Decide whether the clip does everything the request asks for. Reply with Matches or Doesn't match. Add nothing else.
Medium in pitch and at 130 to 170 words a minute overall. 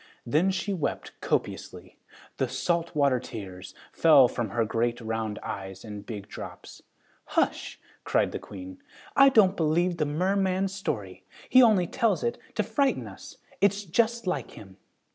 Matches